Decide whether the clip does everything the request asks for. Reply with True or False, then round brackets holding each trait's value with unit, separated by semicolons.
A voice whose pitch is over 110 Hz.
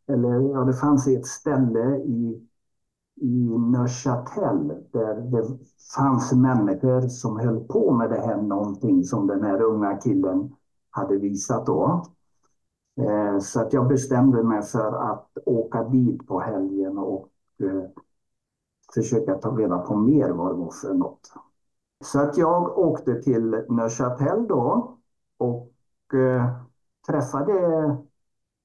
True (125 Hz)